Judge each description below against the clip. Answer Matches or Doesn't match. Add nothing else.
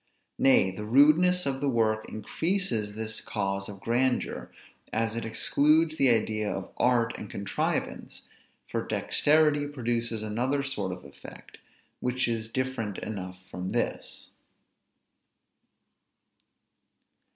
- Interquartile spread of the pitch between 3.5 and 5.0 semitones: Matches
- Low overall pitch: Matches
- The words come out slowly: Matches